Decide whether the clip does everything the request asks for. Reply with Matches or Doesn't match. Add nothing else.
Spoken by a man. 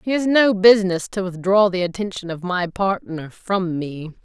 Doesn't match